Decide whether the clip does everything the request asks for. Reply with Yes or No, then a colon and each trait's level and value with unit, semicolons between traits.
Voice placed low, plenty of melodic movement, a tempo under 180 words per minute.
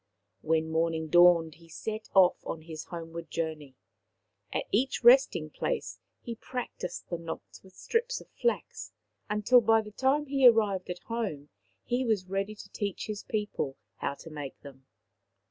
No: high, 190 Hz; wide, 5.8 semitones; average, 160 wpm